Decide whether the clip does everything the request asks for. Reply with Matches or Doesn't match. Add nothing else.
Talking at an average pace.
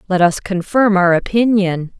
Matches